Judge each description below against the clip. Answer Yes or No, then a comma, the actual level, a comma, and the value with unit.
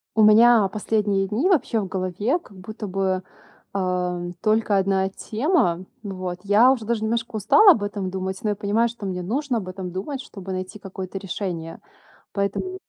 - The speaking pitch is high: Yes, high, 200 Hz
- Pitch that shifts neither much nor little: Yes, average, 3.2 semitones